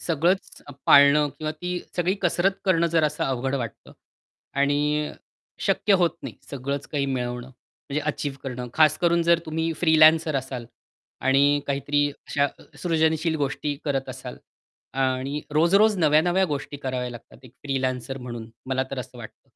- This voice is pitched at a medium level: Yes, medium, 145 Hz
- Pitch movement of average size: Yes, average, 3.3 semitones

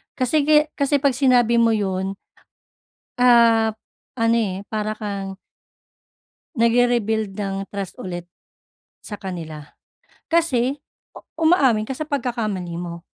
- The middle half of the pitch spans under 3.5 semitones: No, average, 4.4 semitones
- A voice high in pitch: Yes, high, 225 Hz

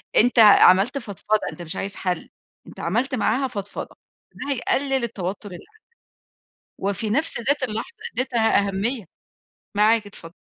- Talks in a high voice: Yes, high, 220 Hz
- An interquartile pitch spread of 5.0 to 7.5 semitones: No, average, 4.6 semitones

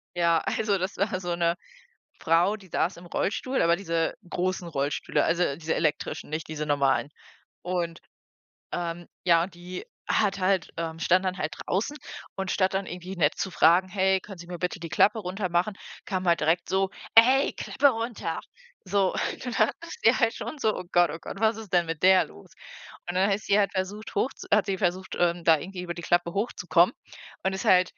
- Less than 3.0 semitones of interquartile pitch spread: Yes, narrow, 2.5 semitones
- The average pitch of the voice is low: No, medium, 180 Hz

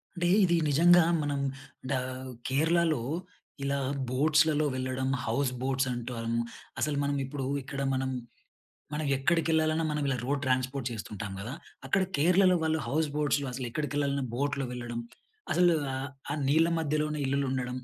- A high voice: No, medium, 140 Hz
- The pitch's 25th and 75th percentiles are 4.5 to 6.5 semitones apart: No, average, 3.2 semitones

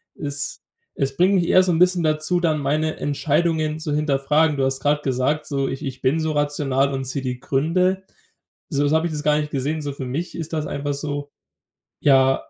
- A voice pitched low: No, medium, 150 Hz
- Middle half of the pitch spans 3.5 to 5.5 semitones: No, narrow, 2.6 semitones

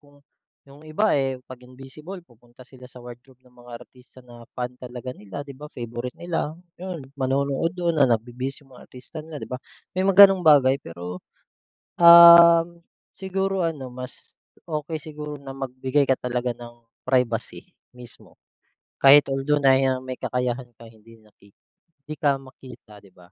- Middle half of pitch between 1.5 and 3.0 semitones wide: No, average, 3.4 semitones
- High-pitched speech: No, low, 130 Hz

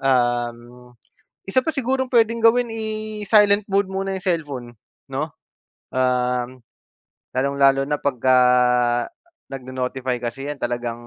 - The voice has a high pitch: No, low, 135 Hz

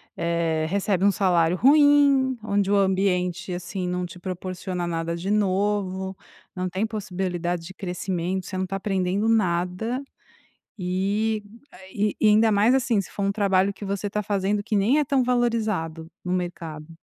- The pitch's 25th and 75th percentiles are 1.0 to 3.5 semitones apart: Yes, average, 2.7 semitones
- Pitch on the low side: No, high, 190 Hz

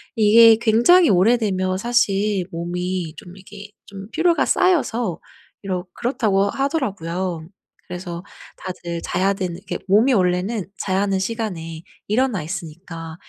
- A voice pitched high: Yes, high, 195 Hz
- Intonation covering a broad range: No, average, 4.0 semitones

